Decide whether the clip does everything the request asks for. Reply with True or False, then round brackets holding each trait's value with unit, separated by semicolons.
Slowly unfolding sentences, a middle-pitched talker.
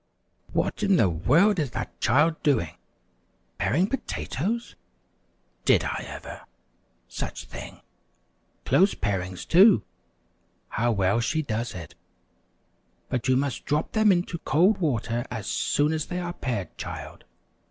True (130 wpm; 145 Hz)